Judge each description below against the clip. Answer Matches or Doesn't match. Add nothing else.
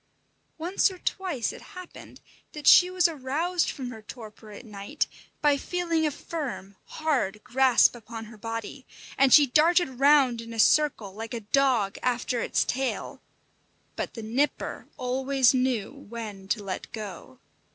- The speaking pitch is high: Matches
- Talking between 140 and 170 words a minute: Matches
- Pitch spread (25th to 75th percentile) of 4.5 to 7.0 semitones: Matches